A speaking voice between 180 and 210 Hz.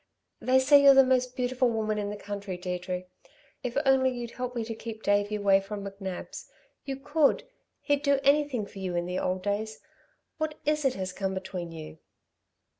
No: high, 220 Hz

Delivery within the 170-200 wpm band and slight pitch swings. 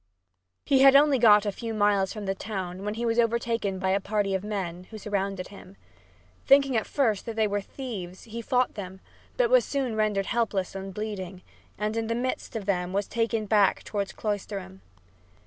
No: average, 195 wpm; average, 3.0 semitones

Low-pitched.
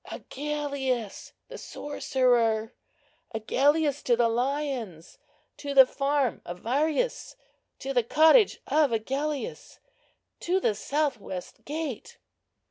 No: very high, 275 Hz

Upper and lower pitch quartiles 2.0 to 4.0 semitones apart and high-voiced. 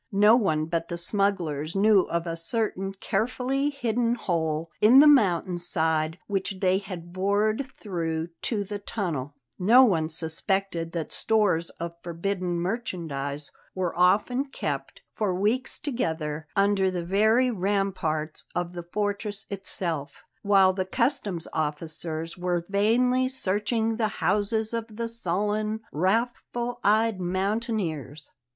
No: average, 4.4 semitones; high, 195 Hz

